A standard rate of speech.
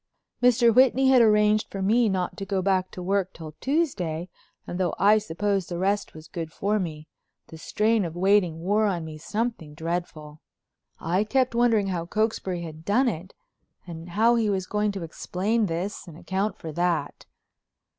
Yes: average, 175 wpm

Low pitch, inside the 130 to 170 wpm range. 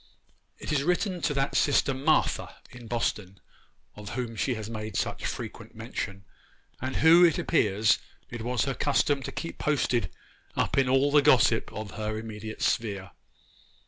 Yes: low, 125 Hz; average, 155 wpm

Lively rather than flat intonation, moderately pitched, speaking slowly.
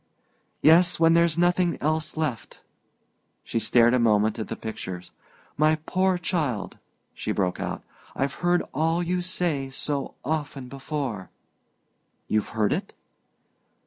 Yes: wide, 6.3 semitones; medium, 150 Hz; slow, 130 wpm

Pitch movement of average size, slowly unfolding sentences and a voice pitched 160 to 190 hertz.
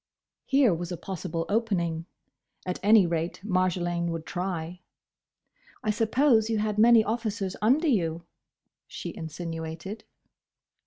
Yes: average, 4.5 semitones; slow, 115 wpm; medium, 185 Hz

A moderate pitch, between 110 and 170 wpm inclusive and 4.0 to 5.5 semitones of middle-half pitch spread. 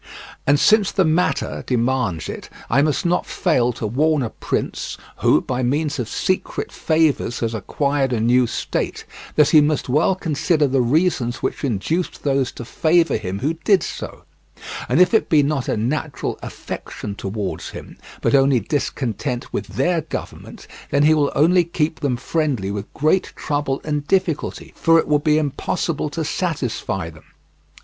Yes: medium, 145 Hz; average, 165 wpm; average, 4.5 semitones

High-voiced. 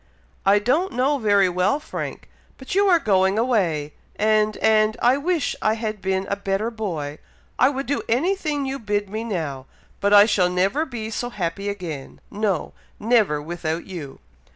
Yes: high, 210 Hz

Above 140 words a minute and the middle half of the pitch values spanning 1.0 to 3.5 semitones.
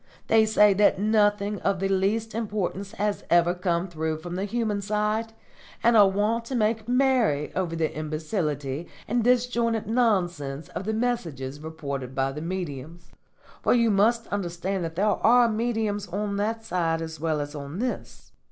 No: average, 165 wpm; average, 5.2 semitones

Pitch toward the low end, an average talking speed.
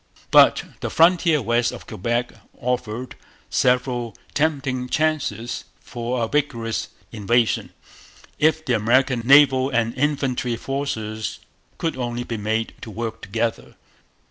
No: low, 120 Hz; slow, 115 wpm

